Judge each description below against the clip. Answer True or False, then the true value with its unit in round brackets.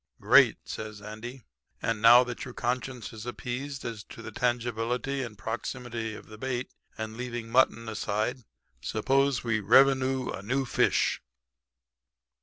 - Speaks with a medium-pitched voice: False (120 Hz)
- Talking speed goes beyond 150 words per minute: False (140 wpm)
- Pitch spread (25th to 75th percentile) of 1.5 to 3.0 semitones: True (2.5 semitones)